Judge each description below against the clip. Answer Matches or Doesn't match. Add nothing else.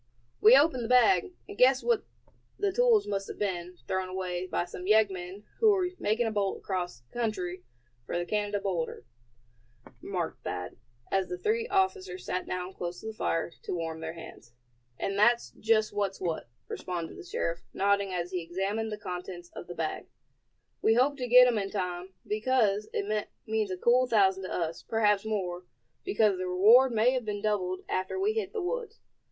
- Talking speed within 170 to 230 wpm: Matches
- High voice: Matches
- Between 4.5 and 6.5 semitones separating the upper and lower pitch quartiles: Matches